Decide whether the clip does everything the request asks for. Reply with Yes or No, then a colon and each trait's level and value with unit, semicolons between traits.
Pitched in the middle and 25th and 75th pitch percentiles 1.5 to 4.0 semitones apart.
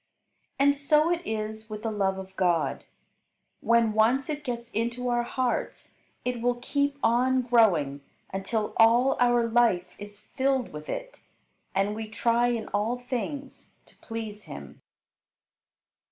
No: high, 235 Hz; average, 2.9 semitones